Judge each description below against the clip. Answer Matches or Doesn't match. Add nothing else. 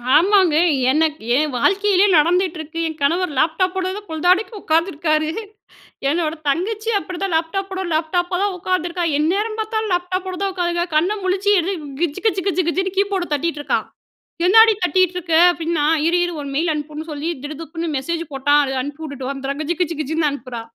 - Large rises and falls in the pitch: Doesn't match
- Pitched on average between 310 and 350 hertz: Matches